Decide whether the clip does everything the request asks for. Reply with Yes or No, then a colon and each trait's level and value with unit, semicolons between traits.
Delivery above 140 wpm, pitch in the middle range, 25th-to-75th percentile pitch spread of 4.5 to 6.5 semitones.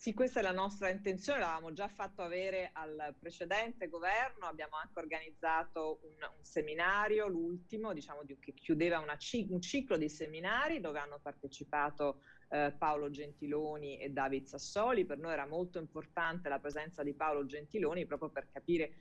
No: average, 160 wpm; medium, 160 Hz; average, 3.9 semitones